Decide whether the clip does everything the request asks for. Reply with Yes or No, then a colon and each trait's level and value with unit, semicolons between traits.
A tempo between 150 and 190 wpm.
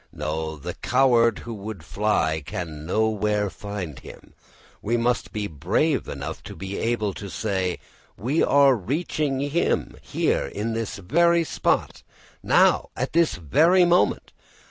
No: average, 140 wpm